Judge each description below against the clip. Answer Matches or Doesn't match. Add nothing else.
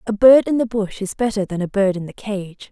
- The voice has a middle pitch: Doesn't match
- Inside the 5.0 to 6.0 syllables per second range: Matches